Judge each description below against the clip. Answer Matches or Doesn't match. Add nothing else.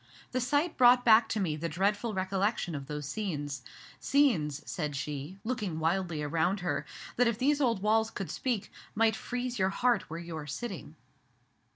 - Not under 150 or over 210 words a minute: Matches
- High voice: Matches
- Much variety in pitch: Matches